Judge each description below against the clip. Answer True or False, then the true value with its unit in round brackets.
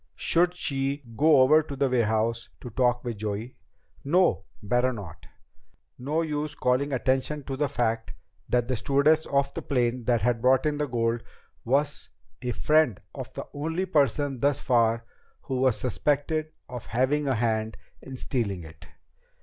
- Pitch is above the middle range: False (130 Hz)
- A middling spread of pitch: True (3.7 semitones)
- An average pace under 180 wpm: True (160 wpm)